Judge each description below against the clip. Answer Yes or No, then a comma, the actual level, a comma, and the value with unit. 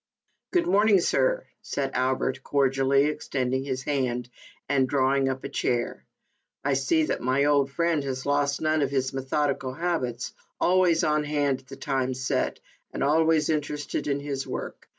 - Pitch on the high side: No, medium, 140 Hz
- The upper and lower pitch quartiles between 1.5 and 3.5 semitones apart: Yes, narrow, 2.4 semitones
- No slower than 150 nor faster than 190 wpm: Yes, average, 170 wpm